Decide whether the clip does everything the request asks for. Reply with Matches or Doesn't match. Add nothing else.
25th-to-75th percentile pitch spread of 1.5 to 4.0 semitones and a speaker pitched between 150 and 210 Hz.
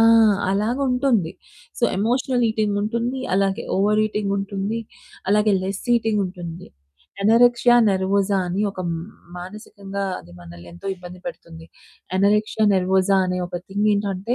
Matches